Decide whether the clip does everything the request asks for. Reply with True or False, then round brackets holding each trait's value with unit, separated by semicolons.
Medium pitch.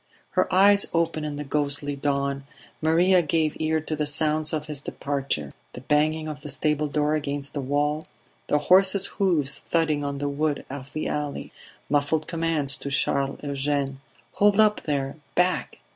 True (150 Hz)